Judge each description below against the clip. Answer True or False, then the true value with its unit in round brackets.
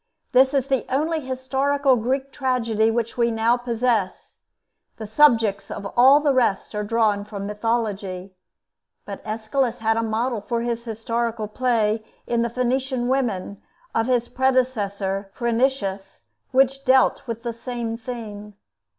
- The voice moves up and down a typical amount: True (3.0 semitones)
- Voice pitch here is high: True (235 Hz)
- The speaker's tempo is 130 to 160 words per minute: True (140 wpm)